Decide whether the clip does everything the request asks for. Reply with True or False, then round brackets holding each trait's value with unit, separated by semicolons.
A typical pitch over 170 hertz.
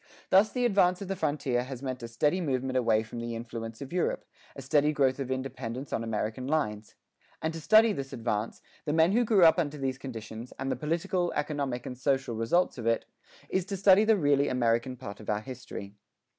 False (135 Hz)